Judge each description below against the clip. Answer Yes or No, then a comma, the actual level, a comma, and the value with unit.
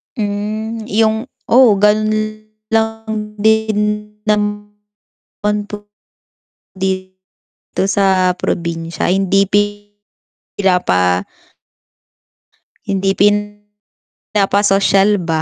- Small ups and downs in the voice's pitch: Yes, narrow, 1.9 semitones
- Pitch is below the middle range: No, high, 205 Hz